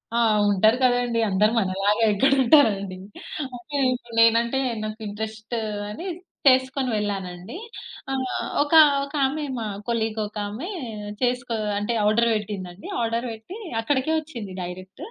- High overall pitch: Yes, high, 225 Hz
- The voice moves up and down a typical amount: Yes, average, 3.6 semitones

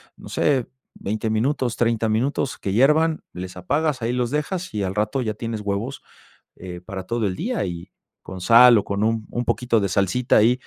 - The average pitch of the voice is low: Yes, low, 115 Hz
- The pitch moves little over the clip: No, average, 4.2 semitones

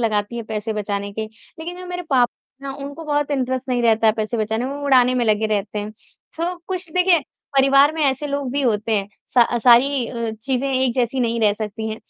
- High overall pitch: Yes, very high, 250 Hz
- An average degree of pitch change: Yes, average, 4.3 semitones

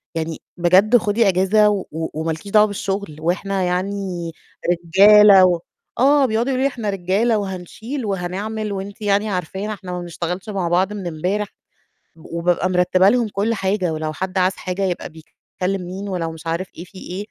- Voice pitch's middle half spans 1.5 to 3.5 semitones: Yes, average, 2.8 semitones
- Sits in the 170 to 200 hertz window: Yes, high, 190 Hz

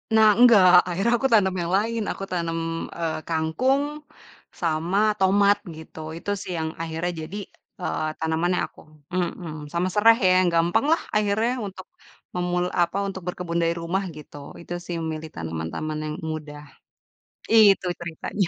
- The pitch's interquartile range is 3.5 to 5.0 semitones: Yes, average, 3.8 semitones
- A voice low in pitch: No, medium, 175 Hz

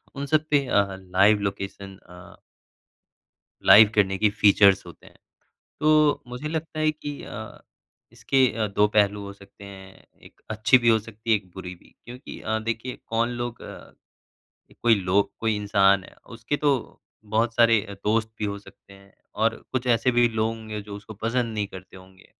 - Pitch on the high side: No, low, 110 Hz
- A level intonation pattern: No, average, 3.2 semitones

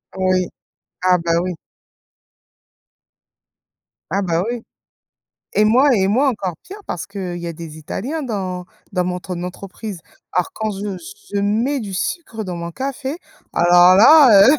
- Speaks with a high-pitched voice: Yes, high, 195 Hz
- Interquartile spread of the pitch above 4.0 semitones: Yes, average, 4.5 semitones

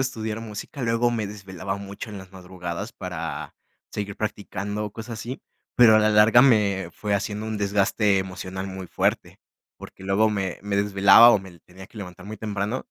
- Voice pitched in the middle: No, low, 100 Hz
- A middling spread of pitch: No, narrow, 2.3 semitones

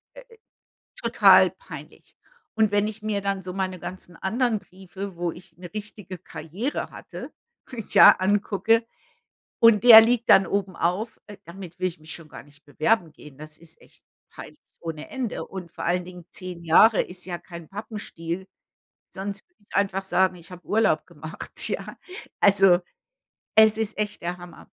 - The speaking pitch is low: No, high, 190 Hz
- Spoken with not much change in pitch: No, average, 3.3 semitones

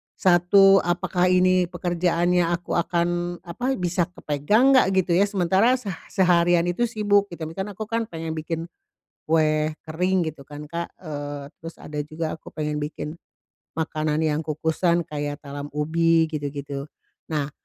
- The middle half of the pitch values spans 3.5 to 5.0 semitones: No, average, 2.9 semitones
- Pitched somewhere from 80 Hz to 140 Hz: No, medium, 170 Hz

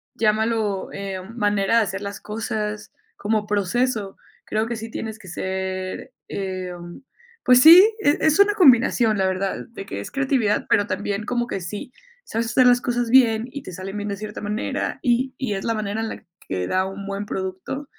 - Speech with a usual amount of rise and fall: Yes, average, 3.6 semitones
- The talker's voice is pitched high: Yes, high, 210 Hz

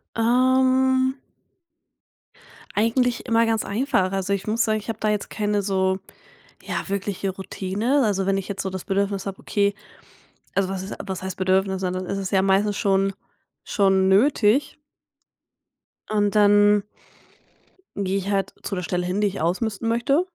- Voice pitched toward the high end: Yes, high, 200 Hz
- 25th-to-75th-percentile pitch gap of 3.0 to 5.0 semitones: No, narrow, 2.5 semitones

